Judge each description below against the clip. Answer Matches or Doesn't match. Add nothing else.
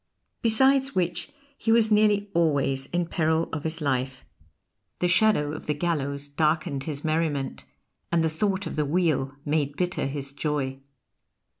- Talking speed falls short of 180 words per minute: Matches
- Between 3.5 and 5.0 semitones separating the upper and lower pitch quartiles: Matches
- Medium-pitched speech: Matches